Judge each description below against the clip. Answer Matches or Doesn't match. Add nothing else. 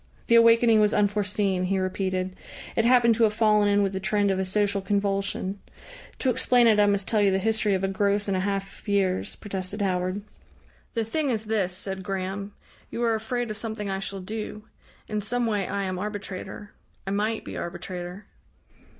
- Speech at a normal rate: Matches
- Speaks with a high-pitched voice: Matches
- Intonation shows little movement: Matches